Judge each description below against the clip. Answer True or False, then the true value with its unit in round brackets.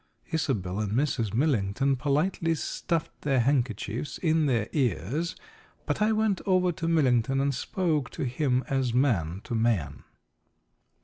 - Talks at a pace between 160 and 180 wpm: False (135 wpm)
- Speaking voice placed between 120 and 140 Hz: True (135 Hz)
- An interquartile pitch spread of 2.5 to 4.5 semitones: False (5.5 semitones)